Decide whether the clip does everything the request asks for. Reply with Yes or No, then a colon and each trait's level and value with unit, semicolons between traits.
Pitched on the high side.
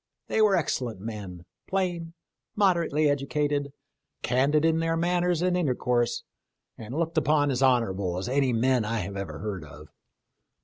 No: medium, 140 Hz